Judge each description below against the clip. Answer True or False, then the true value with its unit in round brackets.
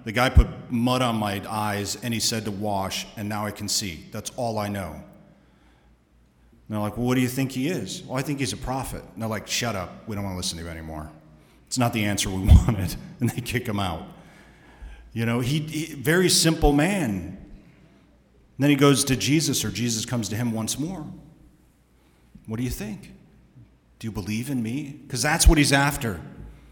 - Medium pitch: False (115 Hz)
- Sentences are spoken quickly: True (215 wpm)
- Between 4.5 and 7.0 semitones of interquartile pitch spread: True (5.3 semitones)